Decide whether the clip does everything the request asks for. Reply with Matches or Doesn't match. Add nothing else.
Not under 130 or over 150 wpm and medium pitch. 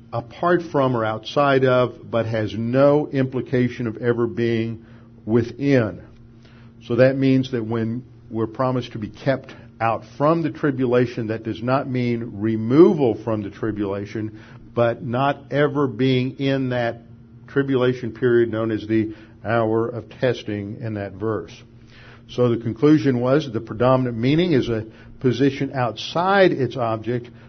Doesn't match